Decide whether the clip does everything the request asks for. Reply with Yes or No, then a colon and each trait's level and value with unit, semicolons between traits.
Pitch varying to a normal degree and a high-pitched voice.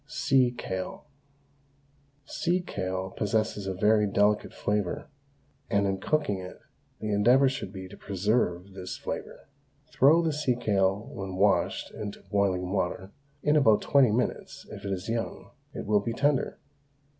No: average, 4.2 semitones; low, 105 Hz